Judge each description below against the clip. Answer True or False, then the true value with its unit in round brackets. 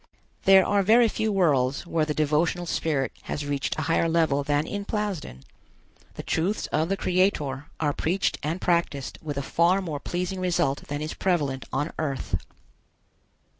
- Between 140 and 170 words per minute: True (165 wpm)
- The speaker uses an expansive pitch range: False (4.1 semitones)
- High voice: False (160 Hz)